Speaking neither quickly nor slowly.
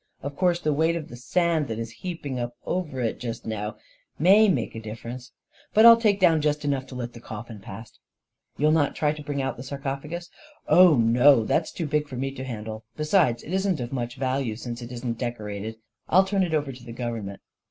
No: fast, 235 wpm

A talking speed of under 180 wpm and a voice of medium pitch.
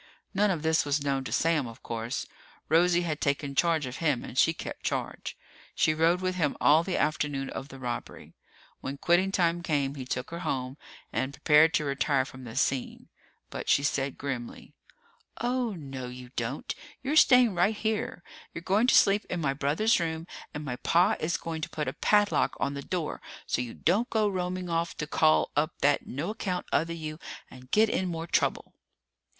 No: average, 195 wpm; medium, 155 Hz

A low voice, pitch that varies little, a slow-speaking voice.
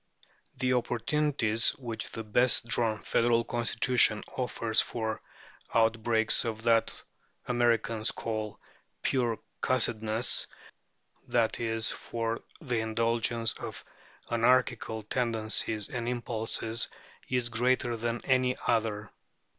Yes: low, 115 Hz; narrow, 1.5 semitones; slow, 100 wpm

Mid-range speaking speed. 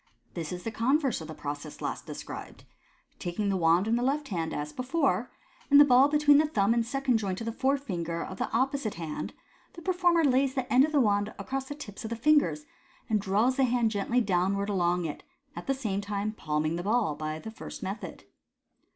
No: fast, 225 wpm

